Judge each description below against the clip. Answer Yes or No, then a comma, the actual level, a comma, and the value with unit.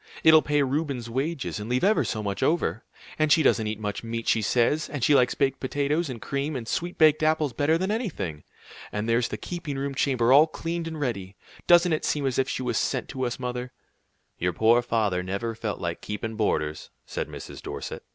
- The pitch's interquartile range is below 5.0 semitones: No, wide, 5.4 semitones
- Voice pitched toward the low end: Yes, low, 130 Hz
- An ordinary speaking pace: No, fast, 210 wpm